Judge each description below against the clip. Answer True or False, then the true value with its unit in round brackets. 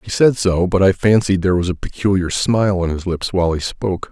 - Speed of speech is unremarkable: False (250 wpm)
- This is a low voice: True (95 Hz)